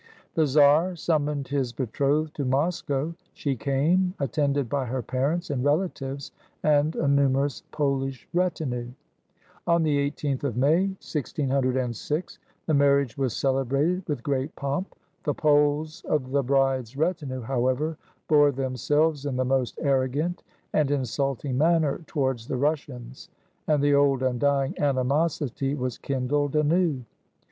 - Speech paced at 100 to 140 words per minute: Yes, slow, 135 wpm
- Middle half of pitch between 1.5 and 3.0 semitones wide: Yes, narrow, 2.5 semitones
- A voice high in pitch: No, medium, 140 Hz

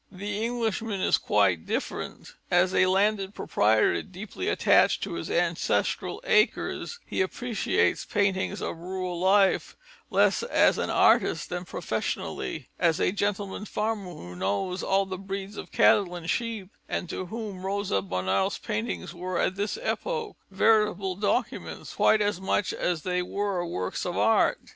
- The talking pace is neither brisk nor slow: Yes, average, 150 wpm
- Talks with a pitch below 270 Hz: Yes, high, 190 Hz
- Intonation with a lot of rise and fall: No, average, 2.8 semitones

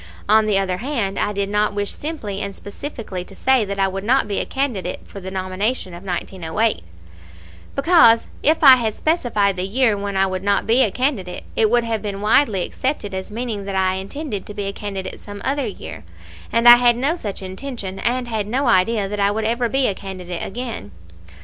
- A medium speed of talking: No, fast, 210 wpm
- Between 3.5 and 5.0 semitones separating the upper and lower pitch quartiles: Yes, average, 3.9 semitones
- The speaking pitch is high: Yes, high, 210 Hz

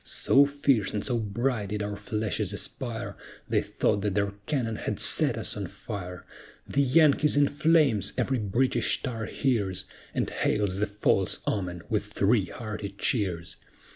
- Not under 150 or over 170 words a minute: Yes, average, 155 wpm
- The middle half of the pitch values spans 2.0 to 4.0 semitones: No, average, 4.5 semitones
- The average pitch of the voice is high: No, low, 105 Hz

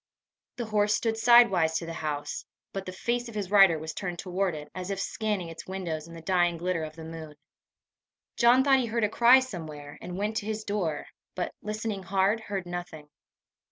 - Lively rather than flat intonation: No, average, 4.6 semitones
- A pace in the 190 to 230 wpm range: Yes, average, 200 wpm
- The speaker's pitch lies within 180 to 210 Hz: Yes, high, 190 Hz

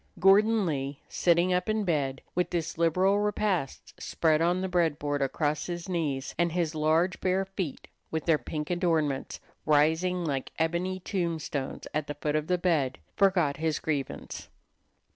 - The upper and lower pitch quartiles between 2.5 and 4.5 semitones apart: Yes, average, 3.4 semitones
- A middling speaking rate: Yes, average, 160 wpm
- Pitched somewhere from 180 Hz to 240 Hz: No, medium, 165 Hz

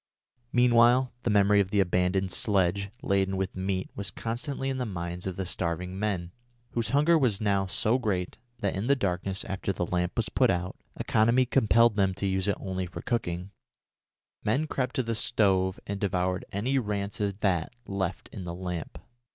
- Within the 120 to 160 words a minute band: No, average, 180 wpm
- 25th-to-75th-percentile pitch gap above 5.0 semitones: No, average, 3.8 semitones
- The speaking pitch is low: Yes, low, 100 Hz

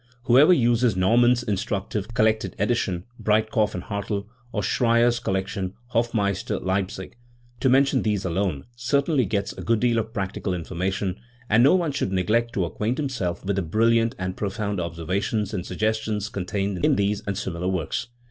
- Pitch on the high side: No, low, 105 Hz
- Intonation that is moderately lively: Yes, average, 3.7 semitones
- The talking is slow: No, average, 165 wpm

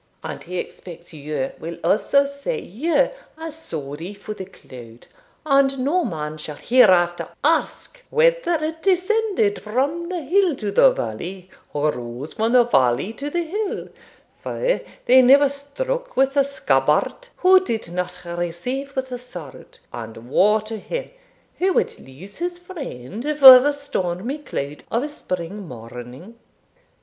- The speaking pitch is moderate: No, high, 245 Hz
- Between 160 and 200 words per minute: No, average, 150 wpm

